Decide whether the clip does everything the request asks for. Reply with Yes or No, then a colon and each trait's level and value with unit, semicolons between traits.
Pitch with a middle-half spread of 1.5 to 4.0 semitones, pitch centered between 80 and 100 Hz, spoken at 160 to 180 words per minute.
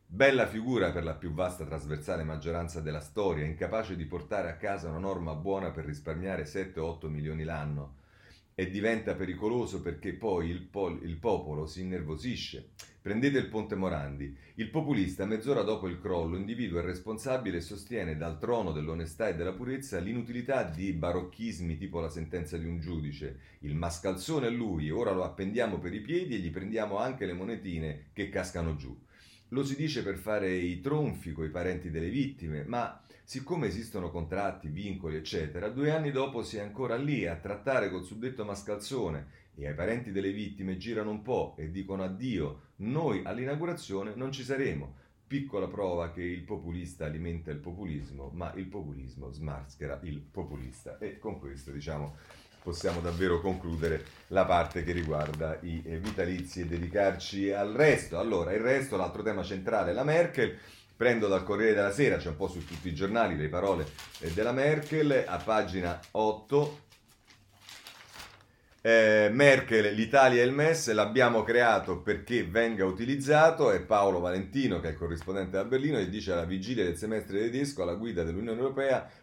No: average, 5.1 semitones; very low, 95 Hz; average, 165 wpm